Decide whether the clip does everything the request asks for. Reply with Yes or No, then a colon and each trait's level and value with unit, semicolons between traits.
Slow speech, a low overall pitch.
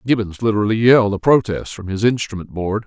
No: average, 190 wpm; low, 105 Hz